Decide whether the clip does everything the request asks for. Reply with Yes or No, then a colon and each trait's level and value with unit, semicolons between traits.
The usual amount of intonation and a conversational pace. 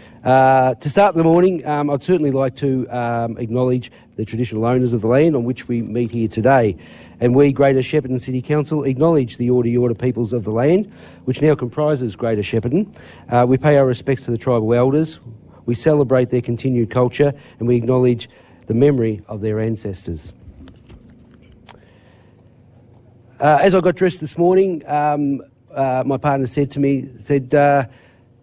Yes: average, 3.3 semitones; average, 170 wpm